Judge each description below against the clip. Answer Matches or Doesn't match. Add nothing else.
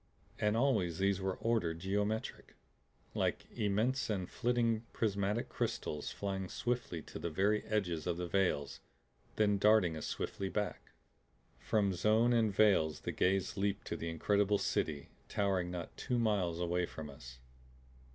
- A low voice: Matches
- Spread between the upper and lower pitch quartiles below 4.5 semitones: Matches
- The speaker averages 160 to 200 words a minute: Doesn't match